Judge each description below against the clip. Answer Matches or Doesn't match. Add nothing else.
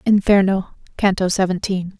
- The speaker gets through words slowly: Matches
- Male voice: Doesn't match